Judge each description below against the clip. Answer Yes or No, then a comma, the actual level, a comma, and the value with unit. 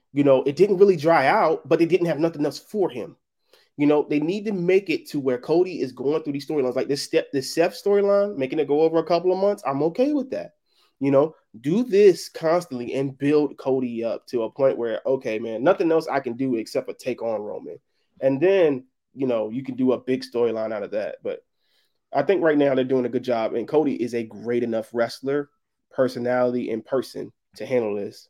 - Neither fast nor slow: No, fast, 230 wpm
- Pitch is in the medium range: Yes, medium, 145 Hz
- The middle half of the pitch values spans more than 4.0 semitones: Yes, average, 5.2 semitones